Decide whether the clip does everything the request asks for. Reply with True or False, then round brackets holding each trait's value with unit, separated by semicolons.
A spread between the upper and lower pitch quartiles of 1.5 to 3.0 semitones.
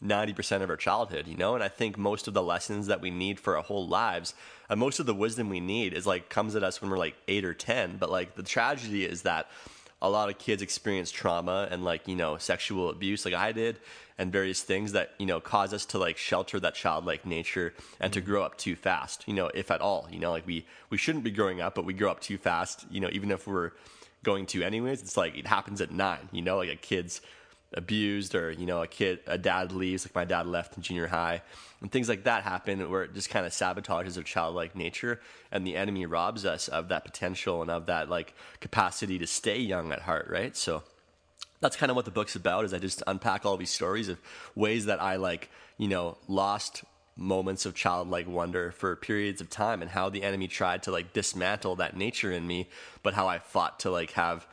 True (2.7 semitones)